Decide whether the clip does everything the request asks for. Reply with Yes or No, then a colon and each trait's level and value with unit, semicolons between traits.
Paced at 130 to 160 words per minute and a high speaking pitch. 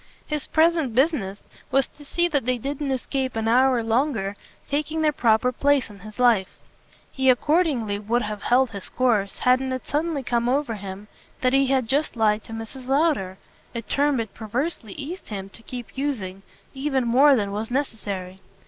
No: average, 175 wpm; very high, 250 Hz